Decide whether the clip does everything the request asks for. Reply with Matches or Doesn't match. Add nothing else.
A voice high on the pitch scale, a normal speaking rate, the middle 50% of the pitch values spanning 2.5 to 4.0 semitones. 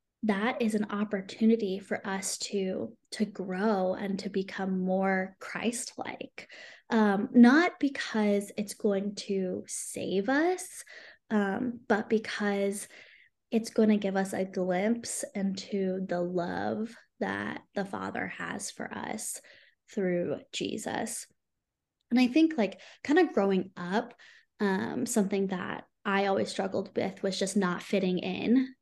Doesn't match